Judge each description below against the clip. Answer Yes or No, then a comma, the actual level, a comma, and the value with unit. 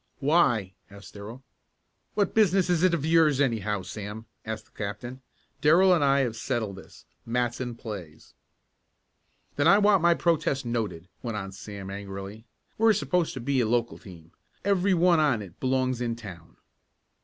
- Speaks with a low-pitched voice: Yes, low, 120 Hz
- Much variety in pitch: Yes, wide, 7.7 semitones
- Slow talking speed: No, average, 160 wpm